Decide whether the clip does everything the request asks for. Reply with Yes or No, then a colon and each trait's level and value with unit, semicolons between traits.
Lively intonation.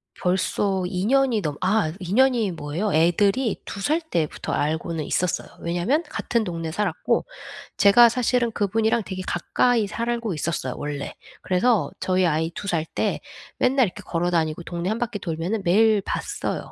No: average, 5.0 semitones